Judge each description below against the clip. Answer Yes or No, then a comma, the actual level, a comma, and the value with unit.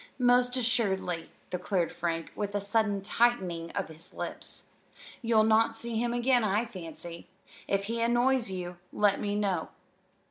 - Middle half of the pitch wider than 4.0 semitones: Yes, average, 4.4 semitones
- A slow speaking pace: No, average, 145 wpm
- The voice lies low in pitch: No, high, 210 Hz